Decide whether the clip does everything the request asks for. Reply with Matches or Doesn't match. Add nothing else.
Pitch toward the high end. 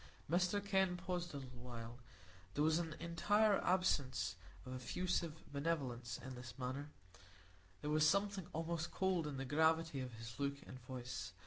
Doesn't match